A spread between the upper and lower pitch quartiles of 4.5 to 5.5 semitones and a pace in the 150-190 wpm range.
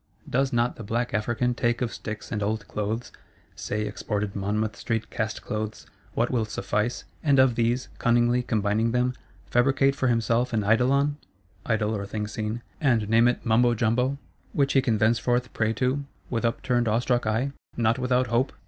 No: narrow, 2.4 semitones; average, 170 wpm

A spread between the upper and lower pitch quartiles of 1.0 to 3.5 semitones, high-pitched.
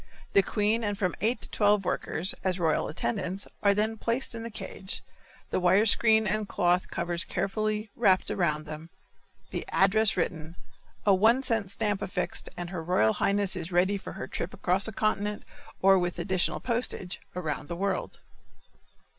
Yes: average, 3.2 semitones; high, 195 Hz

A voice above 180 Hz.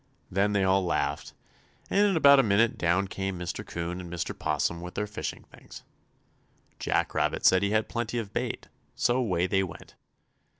No: very low, 95 Hz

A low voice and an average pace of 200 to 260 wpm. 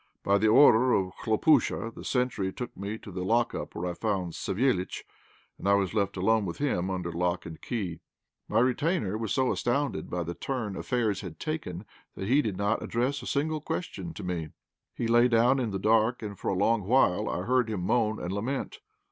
Yes: low, 110 Hz; fast, 205 wpm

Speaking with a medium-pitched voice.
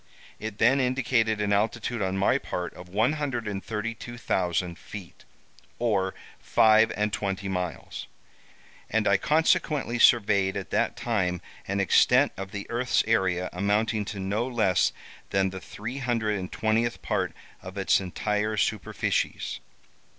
No: low, 105 Hz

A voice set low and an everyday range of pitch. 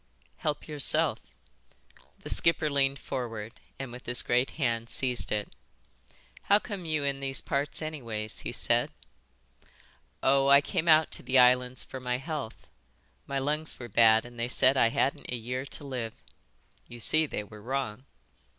Yes: low, 130 Hz; average, 3.0 semitones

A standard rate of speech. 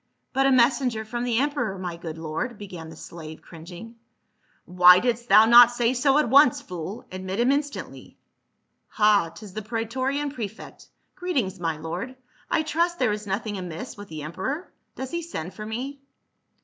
Yes: average, 180 wpm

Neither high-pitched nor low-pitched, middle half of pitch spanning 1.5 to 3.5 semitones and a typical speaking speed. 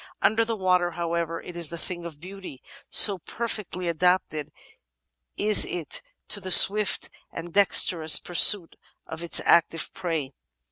Yes: medium, 175 Hz; average, 2.7 semitones; average, 145 wpm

